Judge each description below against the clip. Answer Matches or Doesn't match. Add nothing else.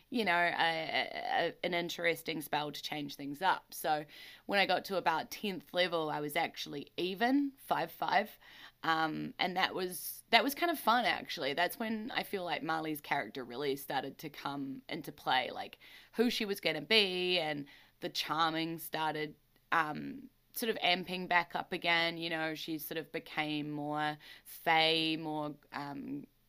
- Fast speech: Doesn't match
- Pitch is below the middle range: Doesn't match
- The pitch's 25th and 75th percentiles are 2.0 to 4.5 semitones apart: Matches